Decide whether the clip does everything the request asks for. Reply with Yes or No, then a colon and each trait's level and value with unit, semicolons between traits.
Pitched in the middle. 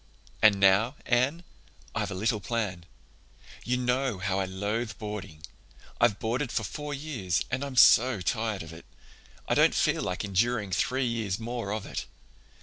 No: low, 110 Hz